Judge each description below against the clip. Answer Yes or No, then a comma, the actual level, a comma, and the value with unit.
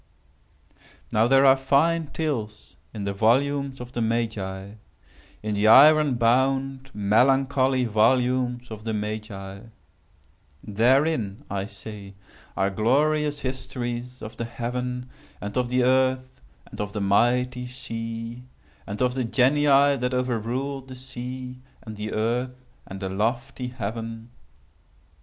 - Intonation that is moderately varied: Yes, average, 3.3 semitones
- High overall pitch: No, low, 125 Hz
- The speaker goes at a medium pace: No, slow, 125 wpm